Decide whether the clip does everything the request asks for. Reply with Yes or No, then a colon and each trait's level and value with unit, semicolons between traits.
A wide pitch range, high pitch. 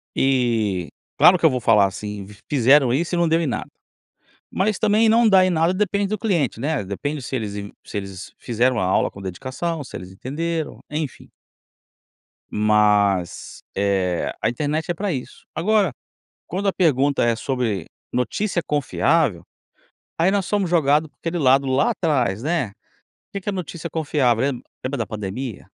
No: wide, 7.6 semitones; medium, 140 Hz